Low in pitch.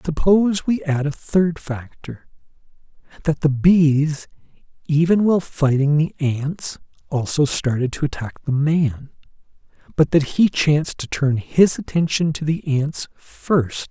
No: medium, 150 Hz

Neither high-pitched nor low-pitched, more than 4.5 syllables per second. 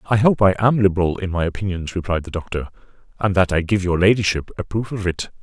No: very low, 95 Hz; 6.3 syllables/s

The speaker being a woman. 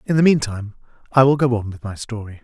No: male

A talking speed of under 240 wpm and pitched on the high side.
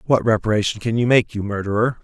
No: fast, 205 wpm; low, 110 Hz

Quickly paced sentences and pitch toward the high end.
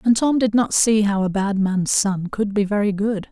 Yes: fast, 255 wpm; high, 205 Hz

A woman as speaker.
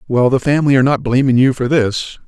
No: male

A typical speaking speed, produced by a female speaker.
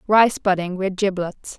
Yes: average, 150 wpm; female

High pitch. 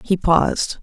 No: medium, 175 Hz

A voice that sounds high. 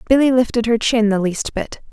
Yes: high, 230 Hz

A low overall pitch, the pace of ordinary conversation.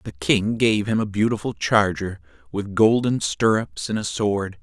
Yes: low, 105 Hz; average, 170 wpm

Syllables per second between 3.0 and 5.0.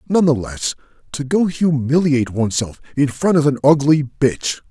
No: 5.4 syllables/s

